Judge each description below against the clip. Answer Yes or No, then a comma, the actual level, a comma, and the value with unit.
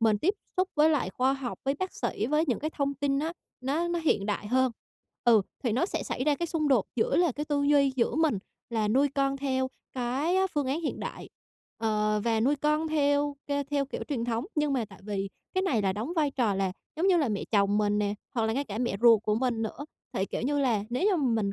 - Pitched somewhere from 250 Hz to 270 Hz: Yes, very high, 265 Hz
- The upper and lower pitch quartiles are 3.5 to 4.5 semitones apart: No, average, 5.0 semitones